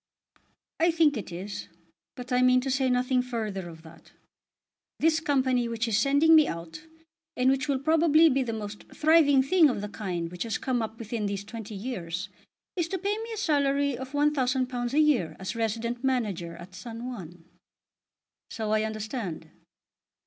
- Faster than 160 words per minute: Yes, average, 175 wpm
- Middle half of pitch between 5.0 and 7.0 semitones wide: Yes, average, 5.3 semitones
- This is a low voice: No, high, 245 Hz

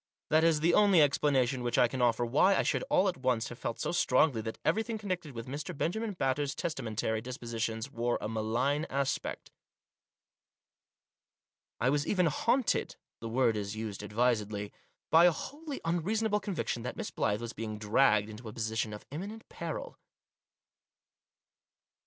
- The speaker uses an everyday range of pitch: No, wide, 6.8 semitones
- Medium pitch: No, low, 130 Hz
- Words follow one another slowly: No, average, 165 wpm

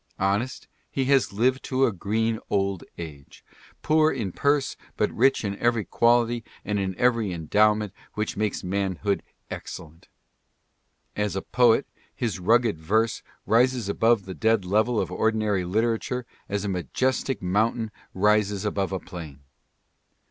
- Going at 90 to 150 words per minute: Yes, average, 140 wpm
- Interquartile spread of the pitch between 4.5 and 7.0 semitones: No, average, 3.5 semitones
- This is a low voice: Yes, low, 105 Hz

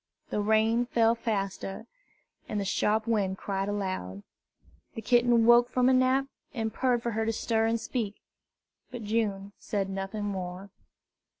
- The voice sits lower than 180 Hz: No, high, 220 Hz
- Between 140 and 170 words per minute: Yes, average, 155 wpm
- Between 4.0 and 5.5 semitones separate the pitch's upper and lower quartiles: No, average, 3.0 semitones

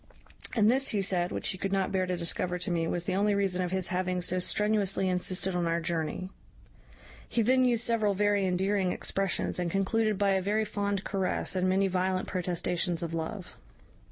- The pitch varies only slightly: Yes, narrow, 2.1 semitones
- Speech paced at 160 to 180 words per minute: No, average, 195 wpm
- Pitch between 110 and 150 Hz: No, high, 190 Hz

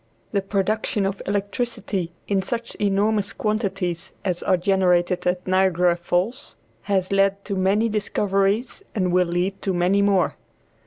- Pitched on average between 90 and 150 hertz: No, high, 195 Hz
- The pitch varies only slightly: Yes, narrow, 2.0 semitones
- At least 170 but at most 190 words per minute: No, average, 140 wpm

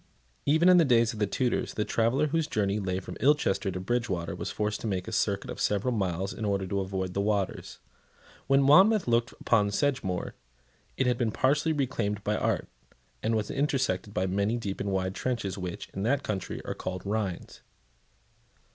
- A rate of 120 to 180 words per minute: No, average, 190 wpm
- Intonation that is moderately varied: Yes, average, 4.8 semitones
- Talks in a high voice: No, low, 105 Hz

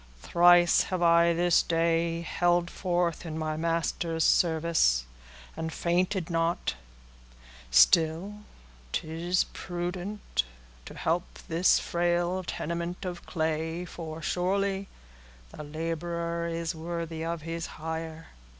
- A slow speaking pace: Yes, slow, 110 wpm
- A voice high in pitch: No, medium, 170 Hz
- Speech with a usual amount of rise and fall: No, narrow, 1.3 semitones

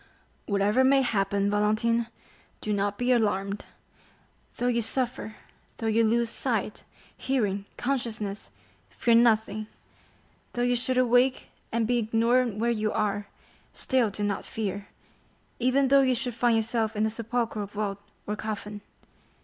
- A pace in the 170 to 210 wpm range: No, average, 140 wpm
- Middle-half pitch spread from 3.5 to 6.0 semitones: No, average, 2.8 semitones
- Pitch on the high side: Yes, high, 225 Hz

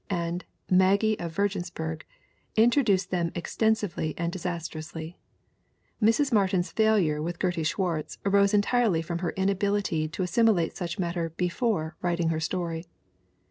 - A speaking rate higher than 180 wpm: No, slow, 135 wpm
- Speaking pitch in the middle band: Yes, medium, 180 Hz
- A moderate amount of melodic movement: Yes, average, 3.2 semitones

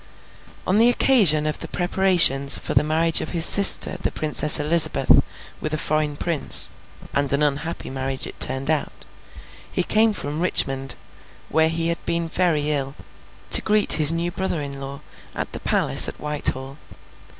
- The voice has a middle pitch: Yes, medium, 155 Hz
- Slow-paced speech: No, average, 165 wpm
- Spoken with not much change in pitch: No, average, 3.3 semitones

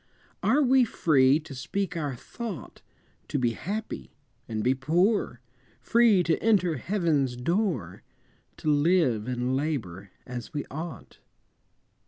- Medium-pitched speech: Yes, medium, 150 Hz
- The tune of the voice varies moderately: No, wide, 6.8 semitones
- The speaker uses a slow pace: Yes, slow, 125 wpm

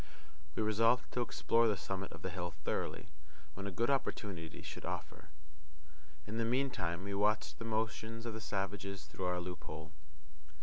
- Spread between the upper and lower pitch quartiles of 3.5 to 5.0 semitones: Yes, average, 3.9 semitones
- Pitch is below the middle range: Yes, low, 100 Hz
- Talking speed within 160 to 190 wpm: Yes, average, 165 wpm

